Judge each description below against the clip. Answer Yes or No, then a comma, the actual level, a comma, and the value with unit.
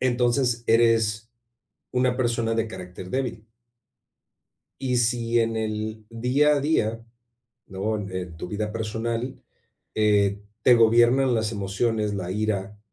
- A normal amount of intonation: No, narrow, 2.2 semitones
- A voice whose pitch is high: No, low, 115 Hz